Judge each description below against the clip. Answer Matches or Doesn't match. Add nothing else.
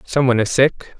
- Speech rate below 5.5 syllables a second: Doesn't match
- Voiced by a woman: Doesn't match